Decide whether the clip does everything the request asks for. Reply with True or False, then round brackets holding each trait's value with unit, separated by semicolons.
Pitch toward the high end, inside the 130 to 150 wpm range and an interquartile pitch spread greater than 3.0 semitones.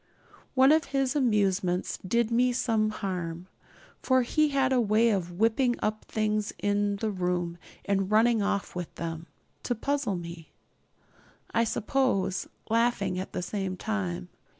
True (210 Hz; 140 wpm; 4.6 semitones)